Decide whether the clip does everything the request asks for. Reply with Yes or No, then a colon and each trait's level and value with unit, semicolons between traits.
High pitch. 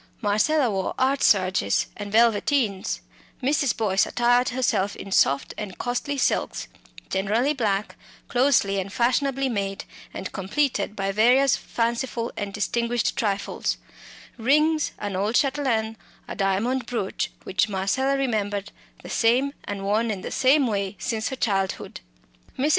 Yes: high, 225 Hz